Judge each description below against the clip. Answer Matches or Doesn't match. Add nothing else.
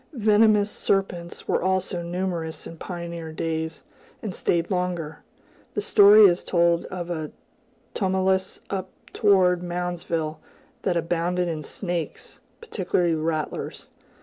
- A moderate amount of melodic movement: Doesn't match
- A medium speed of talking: Doesn't match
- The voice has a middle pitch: Matches